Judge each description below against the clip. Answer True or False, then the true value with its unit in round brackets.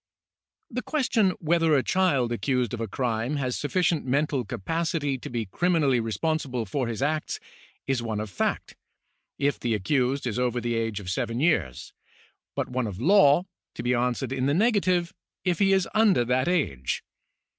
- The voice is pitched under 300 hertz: True (135 Hz)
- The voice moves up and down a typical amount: False (6.1 semitones)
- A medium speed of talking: True (165 wpm)